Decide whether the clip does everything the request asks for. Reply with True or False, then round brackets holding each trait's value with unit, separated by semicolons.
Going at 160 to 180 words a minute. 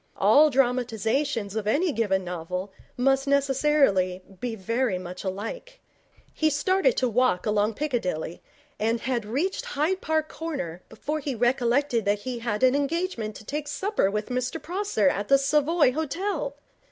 False (150 wpm)